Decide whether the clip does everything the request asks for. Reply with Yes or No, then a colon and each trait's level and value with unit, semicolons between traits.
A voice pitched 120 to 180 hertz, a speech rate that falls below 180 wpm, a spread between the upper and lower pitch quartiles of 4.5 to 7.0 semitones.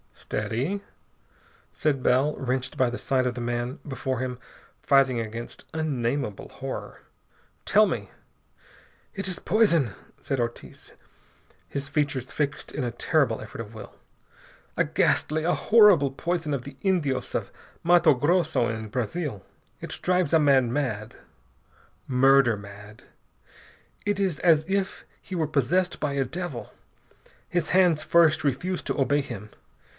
Yes: medium, 140 Hz; average, 140 wpm; average, 5.2 semitones